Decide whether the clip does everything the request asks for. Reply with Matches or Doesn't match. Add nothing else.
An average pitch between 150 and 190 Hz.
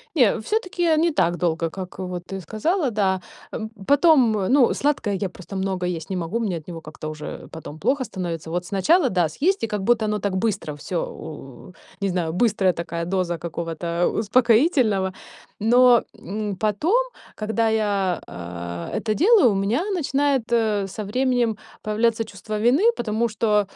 Doesn't match